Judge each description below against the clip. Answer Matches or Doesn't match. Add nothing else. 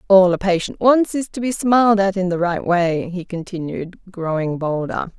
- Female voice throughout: Matches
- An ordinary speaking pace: Matches